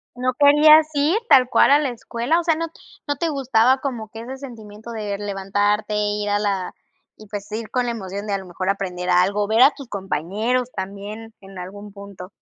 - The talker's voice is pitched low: No, high, 215 Hz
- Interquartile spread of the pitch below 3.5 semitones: No, average, 4.2 semitones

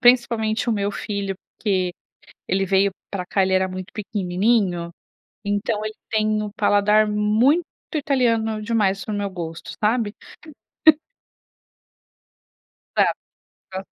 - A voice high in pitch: Yes, high, 210 Hz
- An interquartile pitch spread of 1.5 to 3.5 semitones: Yes, narrow, 2.4 semitones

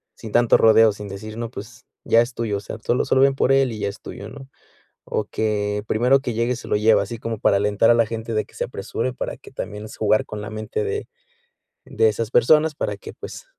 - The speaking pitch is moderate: No, low, 115 Hz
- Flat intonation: Yes, narrow, 2.3 semitones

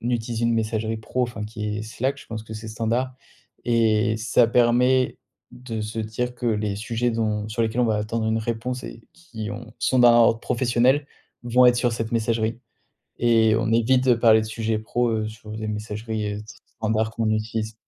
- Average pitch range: No, narrow, 1.7 semitones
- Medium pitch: No, low, 115 Hz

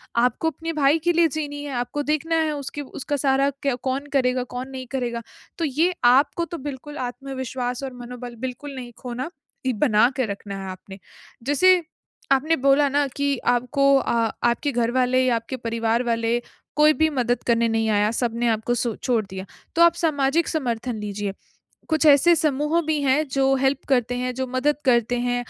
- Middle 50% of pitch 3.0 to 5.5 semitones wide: Yes, average, 3.3 semitones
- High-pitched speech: Yes, very high, 260 Hz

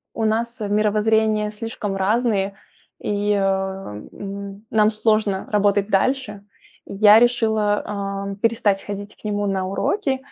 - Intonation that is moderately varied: No, narrow, 1.7 semitones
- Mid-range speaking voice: No, high, 210 Hz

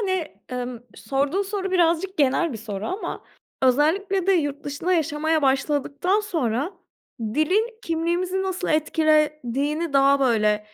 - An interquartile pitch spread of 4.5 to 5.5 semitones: Yes, average, 5.1 semitones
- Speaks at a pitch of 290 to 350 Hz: Yes, very high, 310 Hz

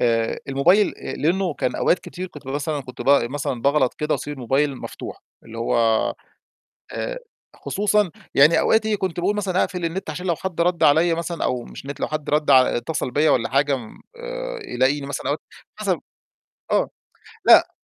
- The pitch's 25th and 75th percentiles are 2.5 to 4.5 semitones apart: No, average, 5.0 semitones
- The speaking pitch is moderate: Yes, medium, 155 Hz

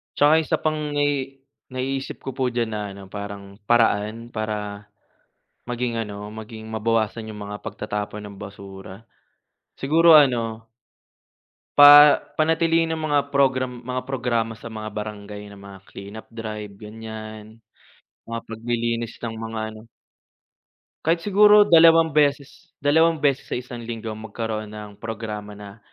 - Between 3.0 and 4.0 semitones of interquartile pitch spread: No, average, 4.4 semitones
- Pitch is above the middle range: No, low, 115 Hz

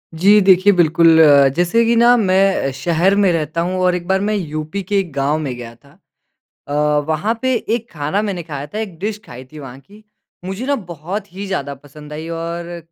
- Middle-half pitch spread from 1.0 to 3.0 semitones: No, average, 4.6 semitones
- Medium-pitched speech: Yes, medium, 175 Hz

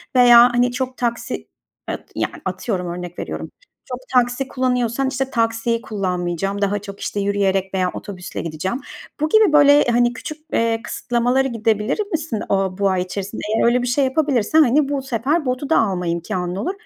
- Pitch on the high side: Yes, high, 235 Hz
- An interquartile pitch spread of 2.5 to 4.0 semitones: No, average, 4.9 semitones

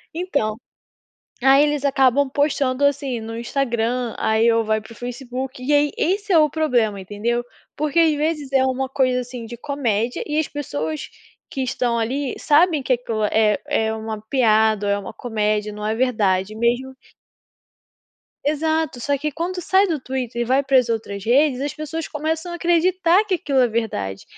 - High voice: Yes, very high, 255 Hz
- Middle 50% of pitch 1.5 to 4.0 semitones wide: No, average, 4.7 semitones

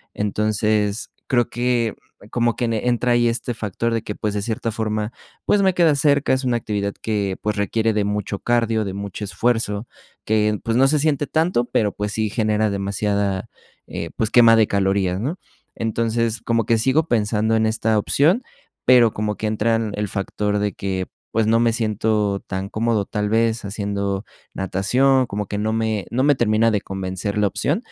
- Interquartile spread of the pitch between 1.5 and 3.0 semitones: Yes, narrow, 2.4 semitones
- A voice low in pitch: Yes, low, 110 Hz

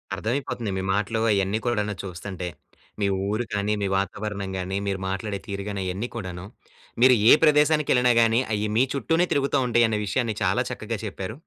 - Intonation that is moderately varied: Yes, average, 3.6 semitones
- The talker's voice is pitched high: No, low, 105 Hz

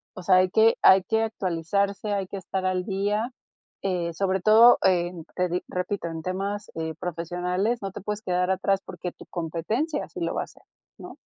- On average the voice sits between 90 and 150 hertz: No, high, 190 Hz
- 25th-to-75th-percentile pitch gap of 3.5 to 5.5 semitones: No, narrow, 2.4 semitones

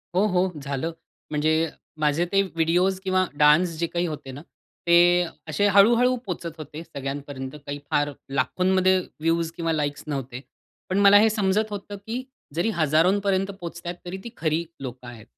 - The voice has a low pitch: No, medium, 170 Hz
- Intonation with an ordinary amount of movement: Yes, average, 4.2 semitones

